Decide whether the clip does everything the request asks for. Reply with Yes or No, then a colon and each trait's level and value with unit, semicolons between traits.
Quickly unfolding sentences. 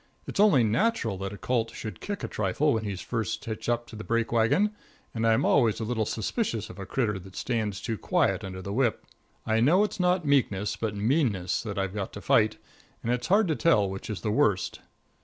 Yes: fast, 220 wpm